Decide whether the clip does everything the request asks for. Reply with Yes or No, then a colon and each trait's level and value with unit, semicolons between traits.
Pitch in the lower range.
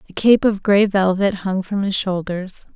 No: high, 195 Hz